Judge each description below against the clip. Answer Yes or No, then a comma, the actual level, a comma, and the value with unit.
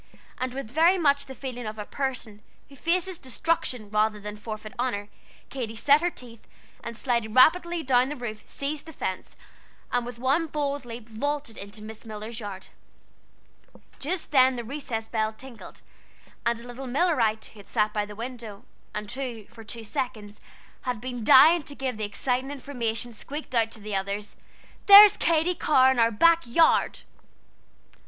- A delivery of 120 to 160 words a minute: No, average, 170 wpm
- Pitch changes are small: No, average, 4.5 semitones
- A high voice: Yes, high, 245 Hz